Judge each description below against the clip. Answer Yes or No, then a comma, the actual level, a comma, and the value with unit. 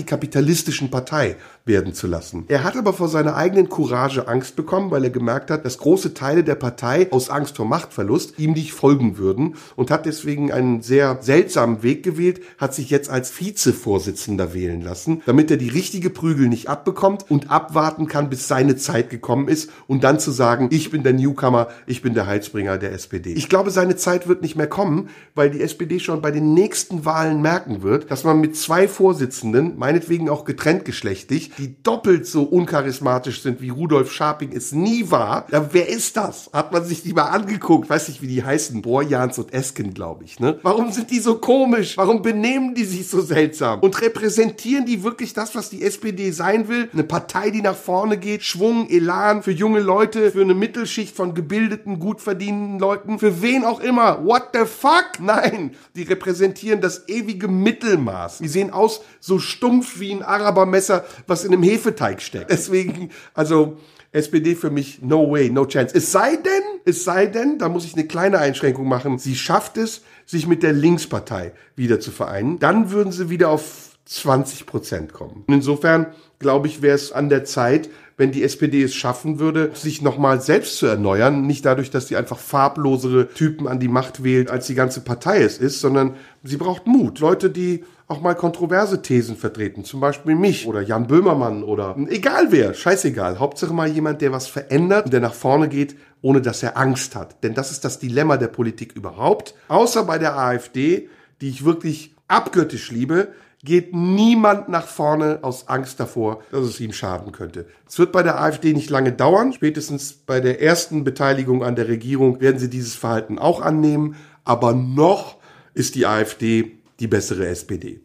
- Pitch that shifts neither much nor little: No, wide, 6.2 semitones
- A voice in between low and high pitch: Yes, medium, 155 Hz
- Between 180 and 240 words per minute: Yes, fast, 190 wpm